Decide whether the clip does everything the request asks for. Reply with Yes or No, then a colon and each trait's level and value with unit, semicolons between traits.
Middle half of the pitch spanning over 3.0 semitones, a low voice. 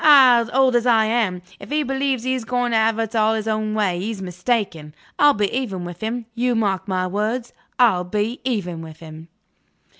No: average, 4.6 semitones; high, 220 Hz